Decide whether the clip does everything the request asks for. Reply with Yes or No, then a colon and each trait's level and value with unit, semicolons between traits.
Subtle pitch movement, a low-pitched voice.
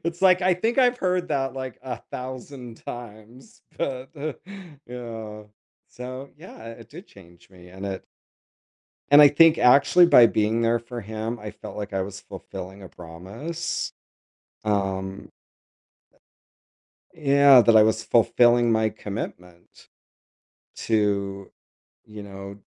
No: average, 5.1 semitones; low, 115 Hz